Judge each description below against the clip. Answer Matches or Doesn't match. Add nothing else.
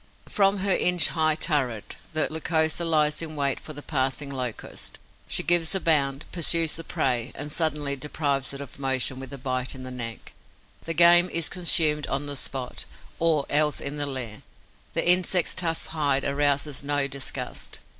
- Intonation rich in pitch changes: Doesn't match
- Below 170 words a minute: Doesn't match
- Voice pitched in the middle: Matches